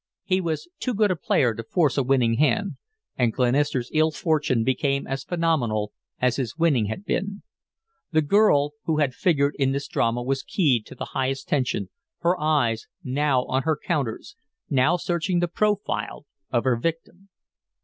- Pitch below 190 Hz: Yes, medium, 140 Hz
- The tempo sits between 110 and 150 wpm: No, average, 165 wpm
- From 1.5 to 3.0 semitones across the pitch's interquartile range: No, average, 4.8 semitones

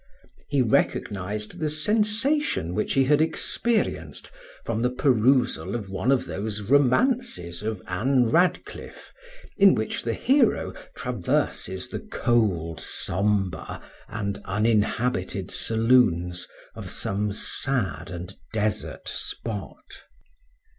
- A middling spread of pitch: No, wide, 6.1 semitones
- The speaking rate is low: Yes, slow, 105 wpm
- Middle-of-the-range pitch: No, low, 110 Hz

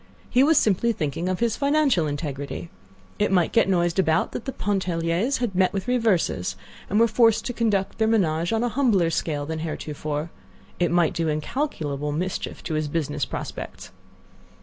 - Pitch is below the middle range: No, medium, 180 Hz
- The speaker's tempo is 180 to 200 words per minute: No, average, 170 wpm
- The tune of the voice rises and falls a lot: Yes, wide, 6.3 semitones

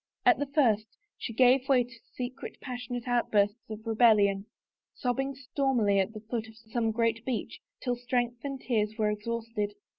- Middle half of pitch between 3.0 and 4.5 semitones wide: No, narrow, 2.6 semitones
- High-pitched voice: Yes, high, 235 Hz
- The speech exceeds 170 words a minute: No, average, 160 wpm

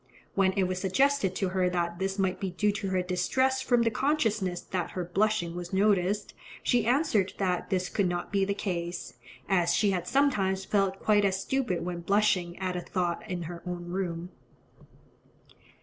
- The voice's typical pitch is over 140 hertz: Yes, high, 190 Hz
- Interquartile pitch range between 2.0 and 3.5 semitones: Yes, narrow, 2.5 semitones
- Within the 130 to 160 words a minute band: No, average, 180 wpm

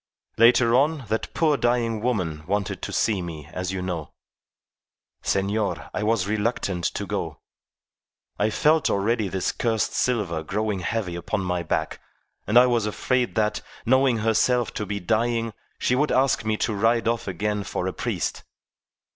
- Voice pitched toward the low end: Yes, low, 110 Hz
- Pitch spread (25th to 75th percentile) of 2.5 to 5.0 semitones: Yes, average, 3.6 semitones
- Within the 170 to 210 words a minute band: No, average, 160 wpm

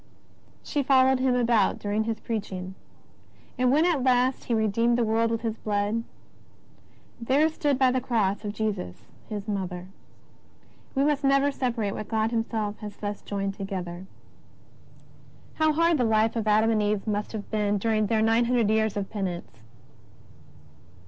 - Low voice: No, high, 220 Hz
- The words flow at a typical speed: Yes, average, 165 wpm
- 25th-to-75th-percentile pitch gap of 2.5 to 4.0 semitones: Yes, average, 3.4 semitones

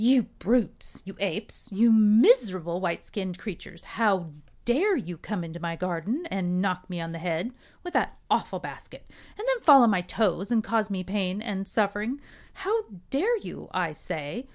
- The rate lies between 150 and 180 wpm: Yes, average, 175 wpm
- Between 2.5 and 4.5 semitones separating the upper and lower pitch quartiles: No, average, 5.0 semitones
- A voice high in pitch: Yes, high, 200 Hz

